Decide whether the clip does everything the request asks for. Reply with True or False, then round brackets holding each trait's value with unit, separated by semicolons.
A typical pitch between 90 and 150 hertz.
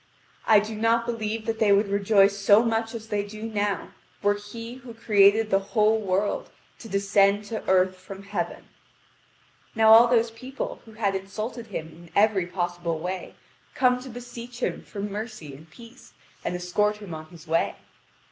False (210 Hz)